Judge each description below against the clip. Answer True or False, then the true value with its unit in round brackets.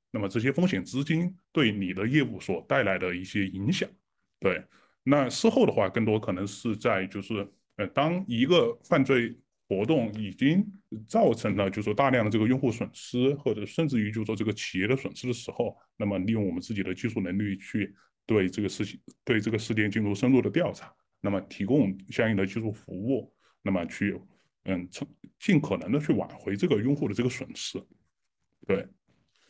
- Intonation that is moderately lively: True (4.6 semitones)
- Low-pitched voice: True (110 Hz)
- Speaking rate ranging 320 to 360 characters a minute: False (285 characters per minute)